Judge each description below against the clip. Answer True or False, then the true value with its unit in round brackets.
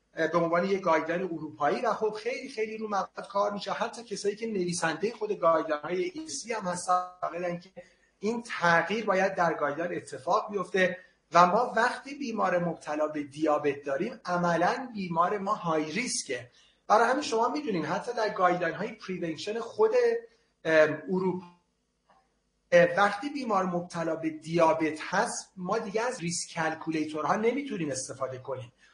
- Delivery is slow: False (140 wpm)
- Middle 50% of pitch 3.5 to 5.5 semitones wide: True (4.9 semitones)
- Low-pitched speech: False (180 Hz)